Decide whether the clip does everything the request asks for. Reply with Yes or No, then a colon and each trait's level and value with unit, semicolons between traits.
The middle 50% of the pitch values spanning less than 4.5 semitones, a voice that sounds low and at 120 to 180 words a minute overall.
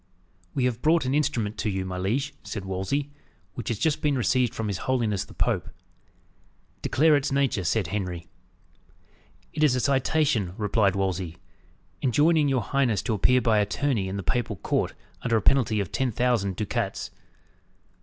No: wide, 5.6 semitones; low, 115 Hz; average, 170 wpm